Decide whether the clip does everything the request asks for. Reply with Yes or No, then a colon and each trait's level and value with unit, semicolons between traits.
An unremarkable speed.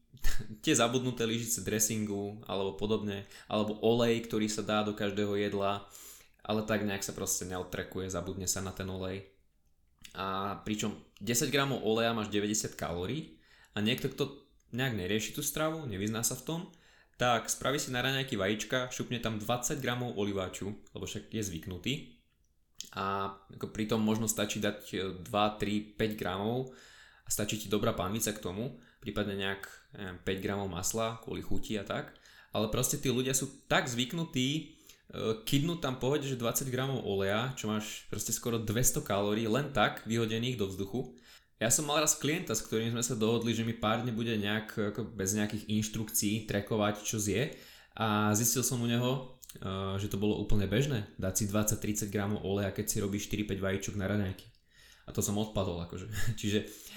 No: fast, 175 wpm